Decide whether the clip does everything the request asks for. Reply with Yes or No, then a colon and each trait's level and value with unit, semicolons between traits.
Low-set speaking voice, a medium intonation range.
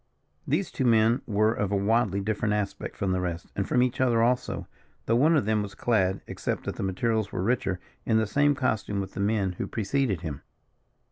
Yes: low, 110 Hz; average, 3.2 semitones